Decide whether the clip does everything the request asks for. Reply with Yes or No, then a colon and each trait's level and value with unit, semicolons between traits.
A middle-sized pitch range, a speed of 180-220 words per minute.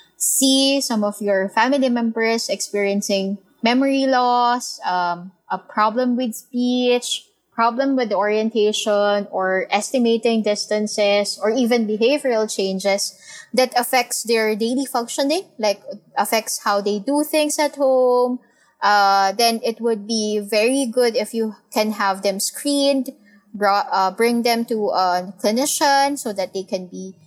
No: average, 3.6 semitones; slow, 135 wpm